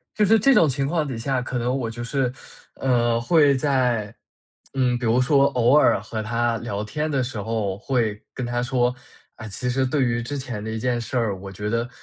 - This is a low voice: Yes, low, 120 Hz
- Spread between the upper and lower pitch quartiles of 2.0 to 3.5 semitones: Yes, average, 2.8 semitones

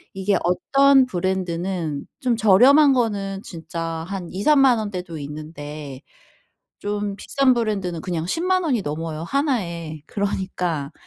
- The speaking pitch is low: No, high, 190 Hz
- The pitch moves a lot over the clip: Yes, wide, 6.1 semitones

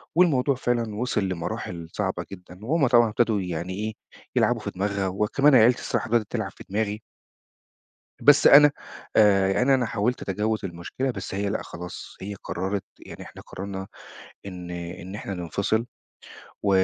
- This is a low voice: Yes, low, 105 Hz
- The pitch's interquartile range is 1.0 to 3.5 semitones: No, average, 4.0 semitones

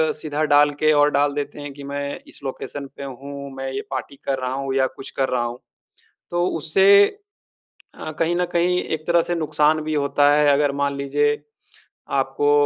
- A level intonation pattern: Yes, narrow, 1.9 semitones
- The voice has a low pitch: No, medium, 145 Hz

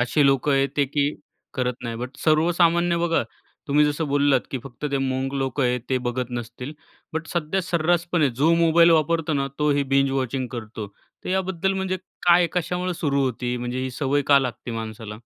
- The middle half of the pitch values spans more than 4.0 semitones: Yes, average, 4.7 semitones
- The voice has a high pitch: No, medium, 140 Hz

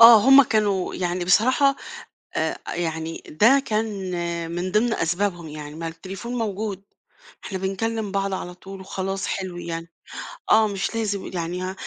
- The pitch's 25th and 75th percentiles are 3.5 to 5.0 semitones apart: Yes, average, 3.8 semitones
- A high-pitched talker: Yes, high, 195 Hz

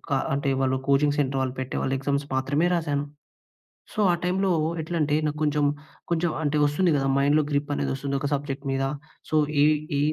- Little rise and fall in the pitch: Yes, narrow, 1.8 semitones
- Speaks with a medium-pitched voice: Yes, medium, 145 Hz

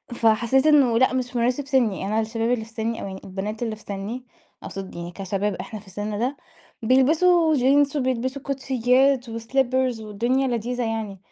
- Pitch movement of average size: Yes, average, 3.5 semitones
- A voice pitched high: Yes, high, 235 Hz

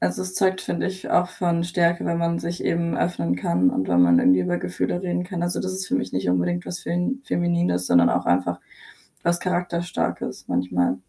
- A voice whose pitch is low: No, medium, 170 Hz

